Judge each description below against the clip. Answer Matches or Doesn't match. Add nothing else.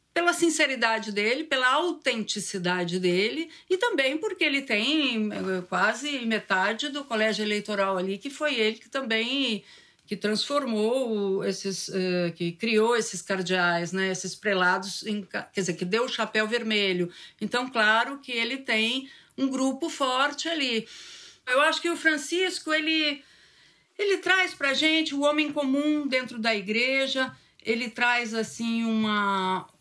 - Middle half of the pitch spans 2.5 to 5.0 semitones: Doesn't match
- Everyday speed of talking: Matches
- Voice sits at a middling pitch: Doesn't match